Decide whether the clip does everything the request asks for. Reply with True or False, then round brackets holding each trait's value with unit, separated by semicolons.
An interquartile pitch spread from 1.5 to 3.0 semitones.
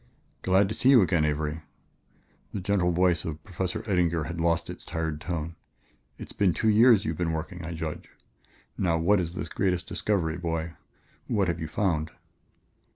True (2.7 semitones)